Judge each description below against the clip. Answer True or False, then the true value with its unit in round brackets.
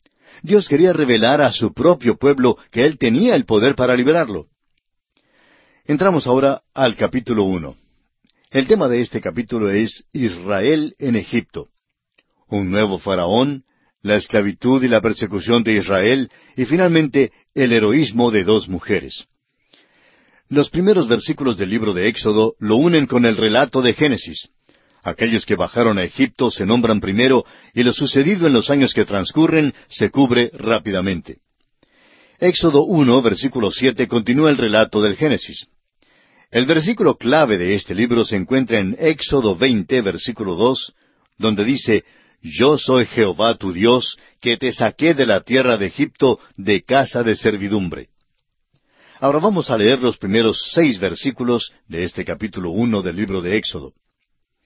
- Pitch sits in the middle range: False (120 Hz)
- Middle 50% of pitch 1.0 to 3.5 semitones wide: False (4.4 semitones)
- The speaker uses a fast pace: False (150 wpm)